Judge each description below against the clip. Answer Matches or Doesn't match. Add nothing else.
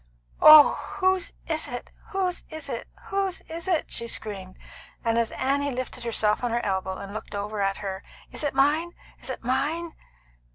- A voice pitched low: Doesn't match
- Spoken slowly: Doesn't match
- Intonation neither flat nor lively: Doesn't match